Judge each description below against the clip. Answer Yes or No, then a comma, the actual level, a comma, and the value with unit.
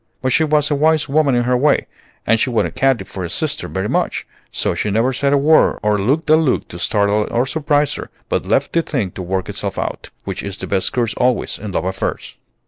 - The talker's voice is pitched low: Yes, low, 125 Hz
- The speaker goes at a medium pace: No, fast, 235 wpm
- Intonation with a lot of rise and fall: Yes, wide, 6.2 semitones